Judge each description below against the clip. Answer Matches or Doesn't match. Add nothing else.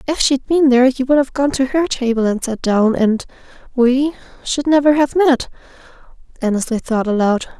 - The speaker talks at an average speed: Matches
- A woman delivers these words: Matches